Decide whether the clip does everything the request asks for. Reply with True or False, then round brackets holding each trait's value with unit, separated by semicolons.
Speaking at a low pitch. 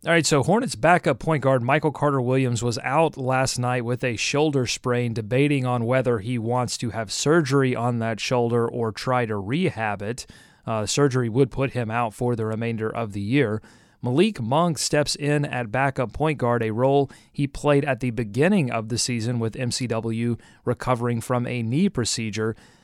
True (125 Hz)